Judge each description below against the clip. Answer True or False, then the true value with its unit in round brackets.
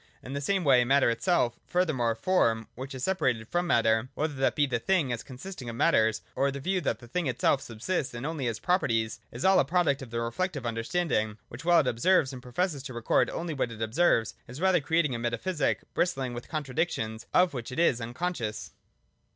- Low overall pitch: True (130 Hz)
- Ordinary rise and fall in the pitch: False (6.4 semitones)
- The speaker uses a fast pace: True (225 wpm)